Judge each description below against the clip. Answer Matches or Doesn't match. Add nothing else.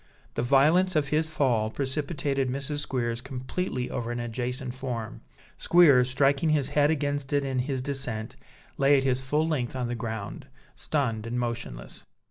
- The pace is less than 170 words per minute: Matches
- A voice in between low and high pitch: Doesn't match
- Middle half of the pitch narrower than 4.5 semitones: Matches